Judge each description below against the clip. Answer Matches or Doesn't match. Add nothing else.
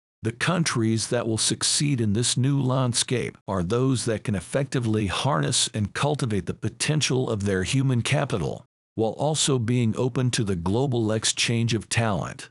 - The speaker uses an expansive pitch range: Doesn't match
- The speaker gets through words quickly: Doesn't match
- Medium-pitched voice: Doesn't match